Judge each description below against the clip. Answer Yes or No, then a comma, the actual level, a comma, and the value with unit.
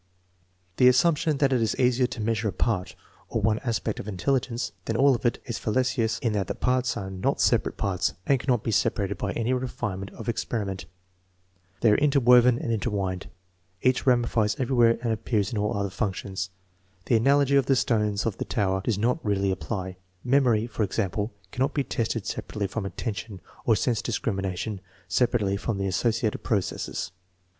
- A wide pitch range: No, average, 3.8 semitones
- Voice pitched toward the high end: No, low, 115 Hz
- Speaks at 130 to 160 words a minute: No, average, 180 wpm